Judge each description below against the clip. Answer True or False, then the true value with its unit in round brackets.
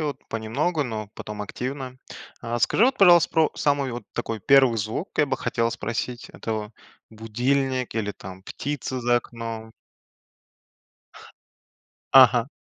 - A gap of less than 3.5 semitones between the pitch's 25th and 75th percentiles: False (3.8 semitones)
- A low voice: True (120 Hz)